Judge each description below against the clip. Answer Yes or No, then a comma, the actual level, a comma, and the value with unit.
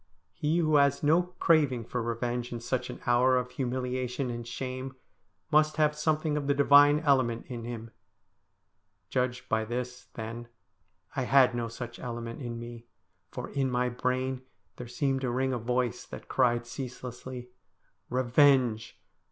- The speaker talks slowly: No, average, 155 wpm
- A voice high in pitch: No, low, 125 Hz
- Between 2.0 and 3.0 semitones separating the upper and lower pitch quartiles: Yes, narrow, 2.4 semitones